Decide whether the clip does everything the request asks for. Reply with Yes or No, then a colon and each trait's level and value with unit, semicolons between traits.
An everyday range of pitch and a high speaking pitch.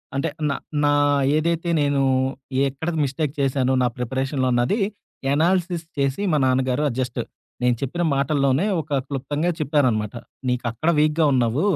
No: average, 3.2 semitones; medium, 140 Hz